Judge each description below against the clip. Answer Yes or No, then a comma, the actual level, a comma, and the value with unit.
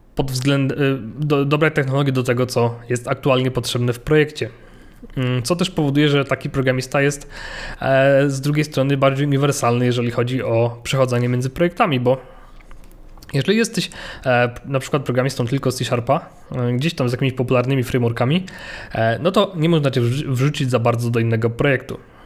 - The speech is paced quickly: Yes, fast, 165 wpm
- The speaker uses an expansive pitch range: No, average, 2.9 semitones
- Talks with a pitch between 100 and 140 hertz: Yes, low, 135 Hz